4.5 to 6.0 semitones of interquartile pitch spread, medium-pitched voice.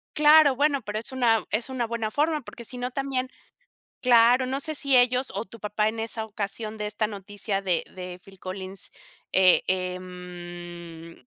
No: average, 5.2 semitones; high, 220 Hz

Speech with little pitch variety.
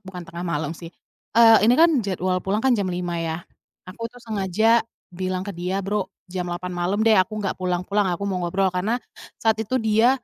No: average, 3.5 semitones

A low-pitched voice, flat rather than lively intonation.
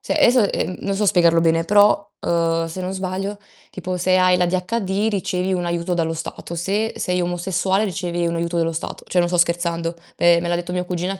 No: medium, 180 Hz; narrow, 1.9 semitones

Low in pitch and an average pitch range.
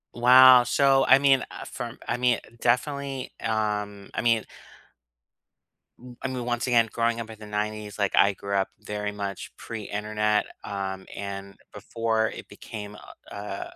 Yes: low, 110 Hz; average, 3.0 semitones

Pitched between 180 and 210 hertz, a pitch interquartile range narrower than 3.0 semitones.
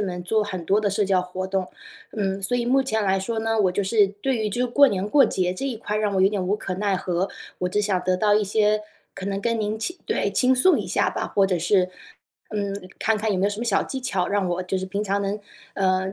Yes: high, 200 Hz; narrow, 2.4 semitones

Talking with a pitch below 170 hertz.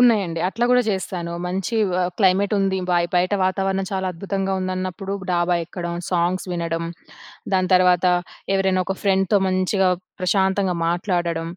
No: medium, 185 Hz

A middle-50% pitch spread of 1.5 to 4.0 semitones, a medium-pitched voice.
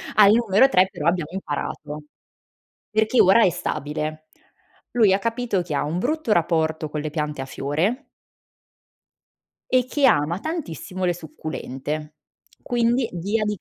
No: wide, 6.6 semitones; medium, 180 Hz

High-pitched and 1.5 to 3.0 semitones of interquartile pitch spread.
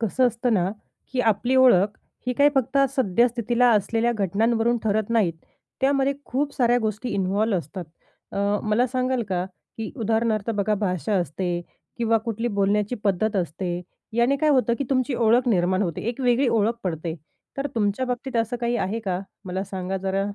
No: high, 225 Hz; average, 4.0 semitones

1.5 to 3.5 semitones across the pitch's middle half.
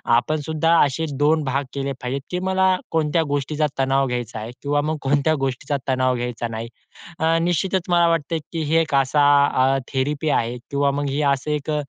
Yes: average, 3.0 semitones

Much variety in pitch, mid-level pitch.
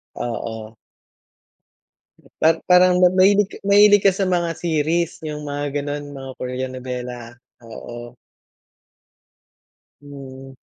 Yes: wide, 5.9 semitones; medium, 145 Hz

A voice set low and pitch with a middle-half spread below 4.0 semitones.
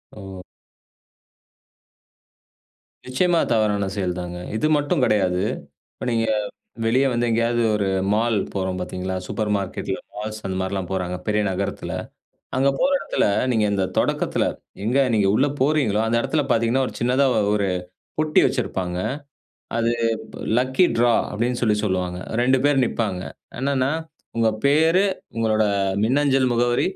No: low, 115 Hz; average, 4.7 semitones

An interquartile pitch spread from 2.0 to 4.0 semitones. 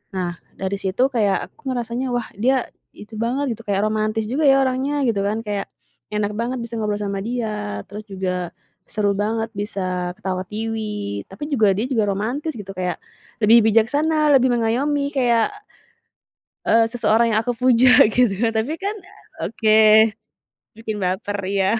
Yes: average, 3.5 semitones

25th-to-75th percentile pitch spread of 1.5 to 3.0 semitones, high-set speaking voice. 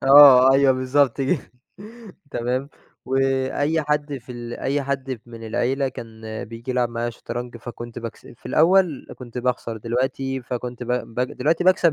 No: narrow, 2.6 semitones; low, 130 Hz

